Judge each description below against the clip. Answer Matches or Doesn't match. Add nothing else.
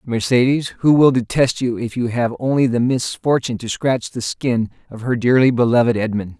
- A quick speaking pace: Doesn't match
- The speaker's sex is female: Doesn't match